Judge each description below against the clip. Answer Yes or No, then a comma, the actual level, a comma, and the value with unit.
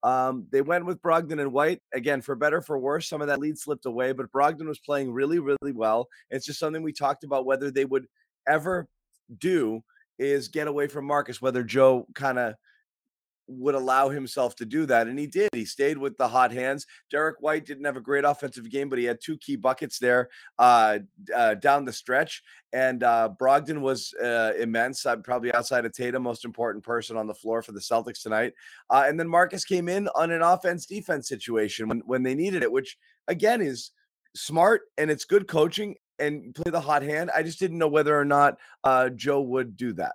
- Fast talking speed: Yes, fast, 210 wpm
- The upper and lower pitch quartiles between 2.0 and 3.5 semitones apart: No, average, 3.9 semitones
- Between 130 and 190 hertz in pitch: Yes, medium, 140 Hz